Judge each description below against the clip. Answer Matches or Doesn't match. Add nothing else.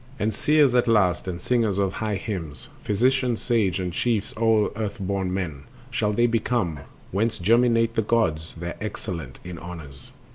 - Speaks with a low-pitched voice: Matches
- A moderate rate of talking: Matches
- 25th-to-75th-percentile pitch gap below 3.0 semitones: Doesn't match